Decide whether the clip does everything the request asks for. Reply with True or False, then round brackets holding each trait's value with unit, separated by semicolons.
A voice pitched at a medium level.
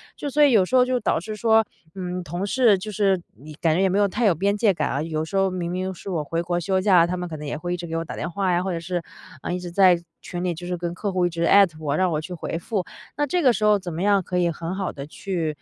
True (180 Hz)